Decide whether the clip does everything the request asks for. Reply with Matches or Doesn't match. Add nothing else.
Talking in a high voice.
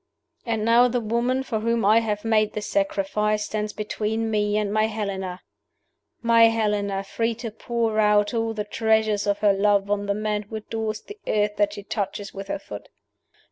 Matches